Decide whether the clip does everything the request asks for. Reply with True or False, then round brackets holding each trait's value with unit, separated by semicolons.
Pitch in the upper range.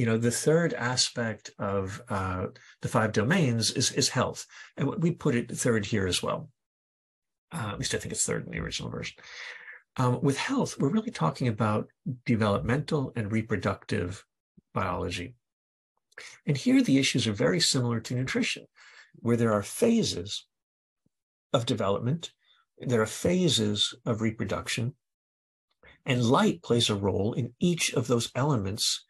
False (120 Hz)